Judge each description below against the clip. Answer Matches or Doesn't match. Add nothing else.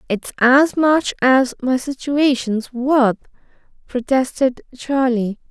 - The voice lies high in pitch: Matches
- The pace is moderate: Doesn't match